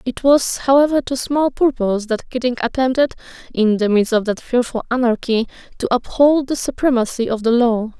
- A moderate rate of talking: Yes, average, 175 wpm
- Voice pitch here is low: No, high, 245 Hz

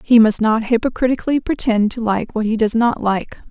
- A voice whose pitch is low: No, high, 225 Hz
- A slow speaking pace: No, fast, 205 wpm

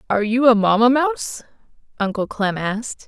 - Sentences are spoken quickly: No, average, 155 wpm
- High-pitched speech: Yes, high, 225 Hz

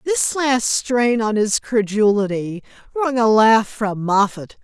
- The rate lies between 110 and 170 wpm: Yes, average, 140 wpm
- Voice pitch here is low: No, high, 225 Hz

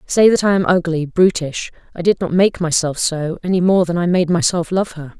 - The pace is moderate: No, fast, 230 wpm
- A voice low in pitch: No, medium, 175 Hz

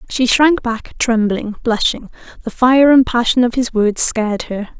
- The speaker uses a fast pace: No, average, 175 wpm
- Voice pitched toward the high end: Yes, high, 235 Hz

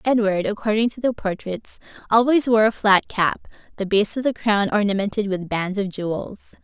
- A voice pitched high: Yes, high, 210 Hz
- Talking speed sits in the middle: Yes, average, 180 wpm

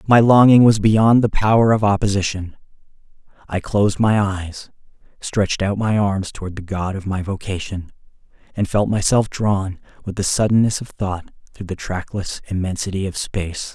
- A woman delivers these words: No, male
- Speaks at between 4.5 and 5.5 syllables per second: Yes, 5.0 syllables/s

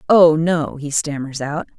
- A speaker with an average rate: Yes, average, 170 wpm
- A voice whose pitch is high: No, medium, 150 Hz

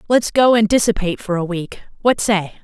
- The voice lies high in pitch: Yes, high, 205 Hz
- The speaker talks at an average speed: Yes, average, 180 wpm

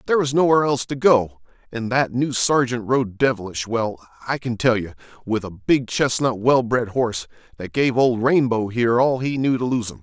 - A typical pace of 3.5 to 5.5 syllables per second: Yes, 5.3 syllables/s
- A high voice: No, low, 120 Hz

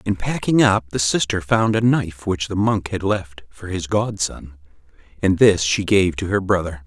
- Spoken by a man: Yes, male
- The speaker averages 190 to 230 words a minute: Yes, average, 200 wpm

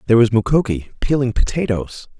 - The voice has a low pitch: Yes, low, 115 Hz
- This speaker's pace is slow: Yes, slow, 110 wpm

